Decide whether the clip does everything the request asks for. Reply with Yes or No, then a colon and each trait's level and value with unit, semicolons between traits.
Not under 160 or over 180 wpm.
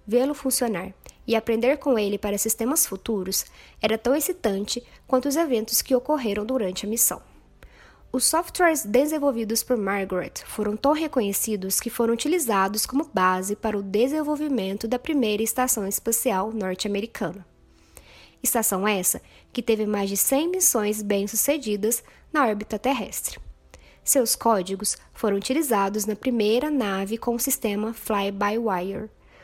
No: average, 130 wpm